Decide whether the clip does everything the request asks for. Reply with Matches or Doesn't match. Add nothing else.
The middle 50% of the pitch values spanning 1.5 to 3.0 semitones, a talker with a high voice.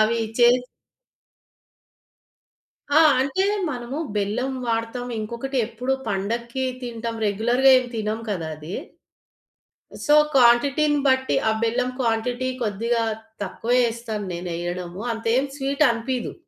Matches